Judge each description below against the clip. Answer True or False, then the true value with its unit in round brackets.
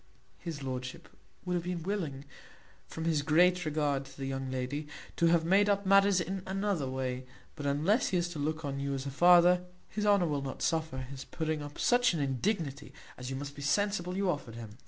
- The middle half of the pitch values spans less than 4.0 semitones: False (4.6 semitones)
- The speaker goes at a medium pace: False (210 wpm)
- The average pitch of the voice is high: False (155 Hz)